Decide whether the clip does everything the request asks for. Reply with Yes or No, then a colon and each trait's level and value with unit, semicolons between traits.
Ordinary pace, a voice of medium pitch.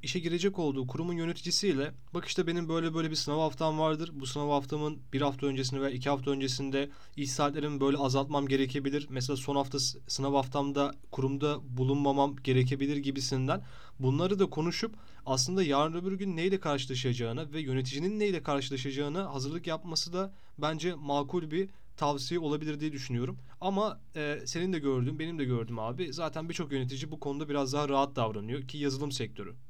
No: fast, 165 wpm; medium, 145 Hz